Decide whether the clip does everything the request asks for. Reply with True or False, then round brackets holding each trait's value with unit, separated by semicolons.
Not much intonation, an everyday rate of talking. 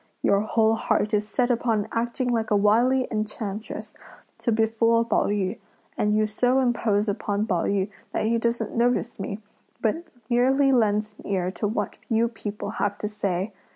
True (2.3 semitones; 170 wpm)